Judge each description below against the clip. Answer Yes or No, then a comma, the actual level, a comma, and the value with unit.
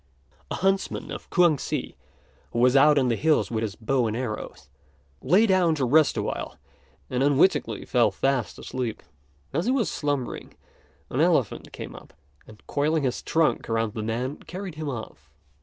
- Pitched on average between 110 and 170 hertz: Yes, low, 135 Hz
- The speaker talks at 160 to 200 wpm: Yes, average, 170 wpm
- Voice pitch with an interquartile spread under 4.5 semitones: No, average, 5.2 semitones